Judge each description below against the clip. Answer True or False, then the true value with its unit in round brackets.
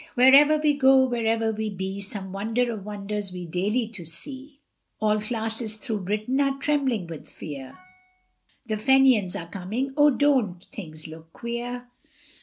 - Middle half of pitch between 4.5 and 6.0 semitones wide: True (5.2 semitones)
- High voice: True (220 Hz)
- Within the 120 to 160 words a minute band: True (150 wpm)